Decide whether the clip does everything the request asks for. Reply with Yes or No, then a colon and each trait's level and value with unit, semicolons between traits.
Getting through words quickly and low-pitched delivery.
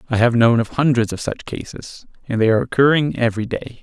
Yes: fast, 220 wpm; low, 120 Hz